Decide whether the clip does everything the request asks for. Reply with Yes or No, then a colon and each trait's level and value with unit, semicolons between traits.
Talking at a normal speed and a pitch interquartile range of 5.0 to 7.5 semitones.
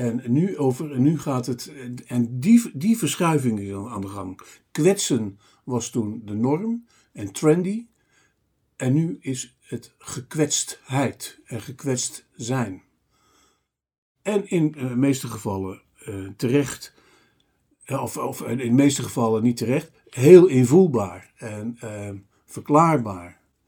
No: slow, 130 wpm; wide, 5.4 semitones